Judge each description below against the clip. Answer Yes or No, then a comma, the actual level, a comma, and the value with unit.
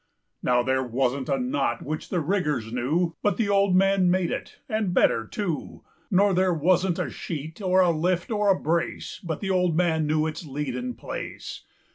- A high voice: No, medium, 170 Hz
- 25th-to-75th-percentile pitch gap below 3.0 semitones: No, average, 4.1 semitones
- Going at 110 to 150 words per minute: No, average, 170 wpm